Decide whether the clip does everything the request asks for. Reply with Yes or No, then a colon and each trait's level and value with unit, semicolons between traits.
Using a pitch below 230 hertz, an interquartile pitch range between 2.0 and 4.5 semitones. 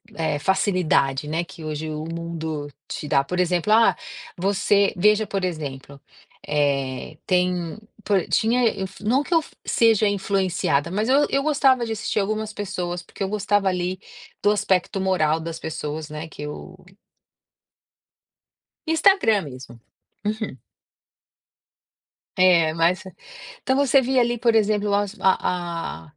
No: medium, 185 Hz; average, 5.0 semitones